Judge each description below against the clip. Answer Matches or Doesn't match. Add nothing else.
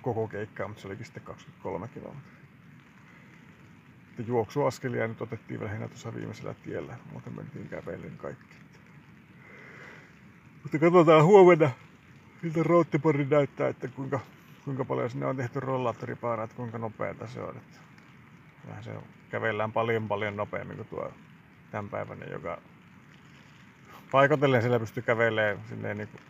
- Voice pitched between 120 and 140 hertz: Matches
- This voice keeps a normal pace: Matches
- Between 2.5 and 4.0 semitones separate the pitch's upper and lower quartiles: Doesn't match